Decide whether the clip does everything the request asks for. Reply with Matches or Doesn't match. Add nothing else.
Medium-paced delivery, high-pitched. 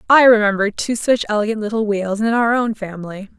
Matches